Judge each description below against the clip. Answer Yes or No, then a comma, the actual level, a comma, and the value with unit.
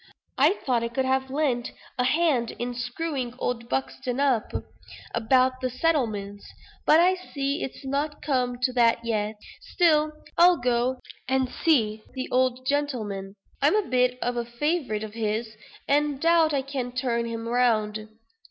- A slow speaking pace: No, average, 160 wpm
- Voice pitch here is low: No, very high, 255 Hz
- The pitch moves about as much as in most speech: Yes, average, 3.4 semitones